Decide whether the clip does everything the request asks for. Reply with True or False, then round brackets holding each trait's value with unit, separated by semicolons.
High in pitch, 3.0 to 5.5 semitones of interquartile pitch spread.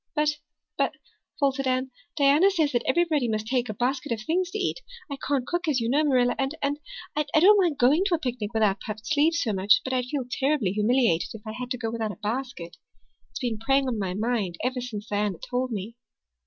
True (255 Hz; 4.7 semitones)